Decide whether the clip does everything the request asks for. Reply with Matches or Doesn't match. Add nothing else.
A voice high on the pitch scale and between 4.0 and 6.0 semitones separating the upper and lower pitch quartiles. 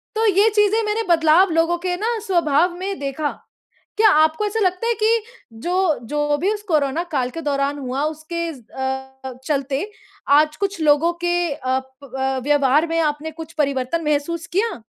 Matches